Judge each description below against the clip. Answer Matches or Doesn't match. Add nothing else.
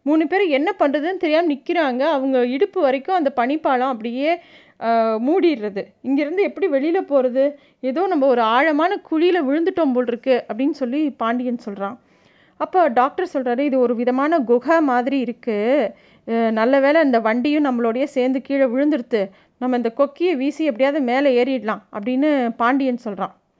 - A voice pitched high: Matches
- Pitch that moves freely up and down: Doesn't match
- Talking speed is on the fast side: Matches